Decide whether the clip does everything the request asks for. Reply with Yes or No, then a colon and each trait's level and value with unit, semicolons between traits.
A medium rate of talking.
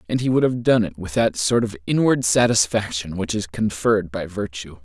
No: fast, 210 wpm